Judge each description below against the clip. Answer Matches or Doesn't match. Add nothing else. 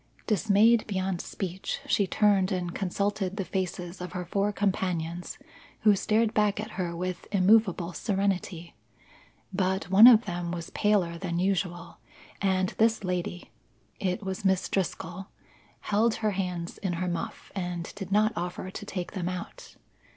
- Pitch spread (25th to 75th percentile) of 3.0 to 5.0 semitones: Doesn't match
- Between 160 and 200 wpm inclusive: Doesn't match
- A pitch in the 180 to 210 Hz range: Matches